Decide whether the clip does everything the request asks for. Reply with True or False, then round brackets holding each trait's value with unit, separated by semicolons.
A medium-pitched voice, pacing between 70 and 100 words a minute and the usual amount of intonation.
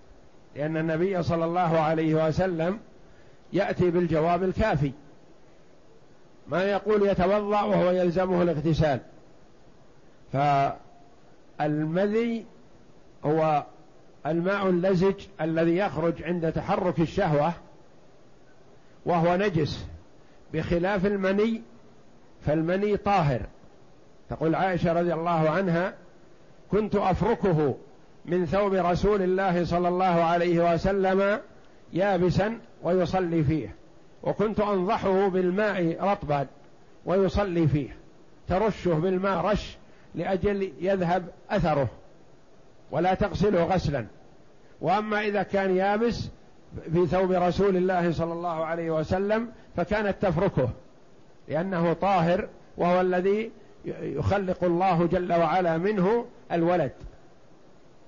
True (180 Hz; 90 wpm; 3.0 semitones)